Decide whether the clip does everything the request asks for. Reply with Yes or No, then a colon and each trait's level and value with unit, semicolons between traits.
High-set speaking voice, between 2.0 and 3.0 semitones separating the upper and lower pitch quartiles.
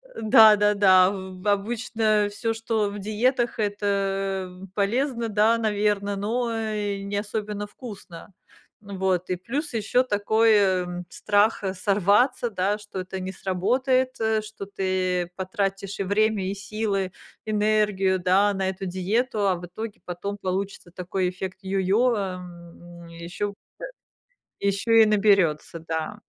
Yes: high, 200 Hz; narrow, 2.4 semitones